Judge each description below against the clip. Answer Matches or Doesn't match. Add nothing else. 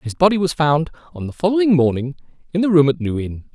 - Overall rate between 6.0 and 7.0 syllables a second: Matches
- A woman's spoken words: Doesn't match